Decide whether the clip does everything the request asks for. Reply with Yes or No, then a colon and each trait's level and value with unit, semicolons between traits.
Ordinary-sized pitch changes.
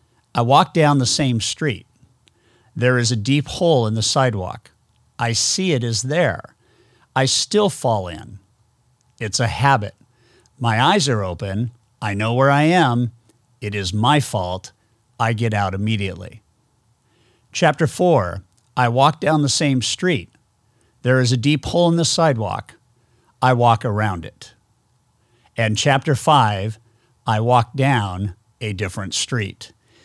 Yes: average, 3.1 semitones